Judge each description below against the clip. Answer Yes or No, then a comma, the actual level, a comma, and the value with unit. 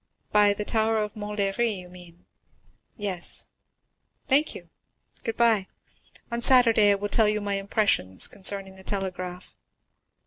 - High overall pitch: Yes, high, 205 Hz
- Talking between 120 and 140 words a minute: Yes, slow, 135 wpm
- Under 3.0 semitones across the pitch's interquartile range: Yes, narrow, 2.5 semitones